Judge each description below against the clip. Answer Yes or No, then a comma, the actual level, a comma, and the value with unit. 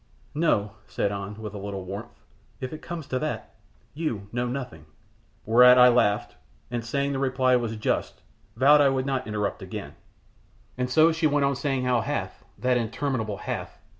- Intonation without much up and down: No, average, 4.3 semitones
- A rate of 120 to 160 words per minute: No, average, 170 wpm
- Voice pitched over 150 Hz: No, low, 125 Hz